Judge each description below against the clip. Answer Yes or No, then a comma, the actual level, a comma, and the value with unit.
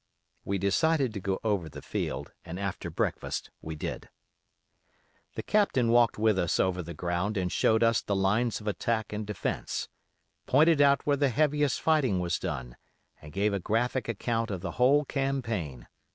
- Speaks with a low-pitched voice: Yes, low, 105 Hz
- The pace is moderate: Yes, average, 170 wpm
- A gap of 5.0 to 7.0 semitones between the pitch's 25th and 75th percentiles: Yes, wide, 5.6 semitones